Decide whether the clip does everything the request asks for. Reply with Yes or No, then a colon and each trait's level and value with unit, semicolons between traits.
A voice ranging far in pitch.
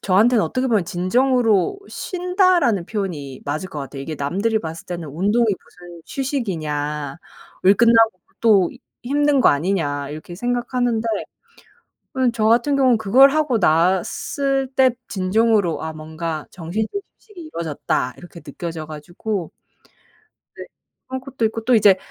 Yes: wide, 6.9 semitones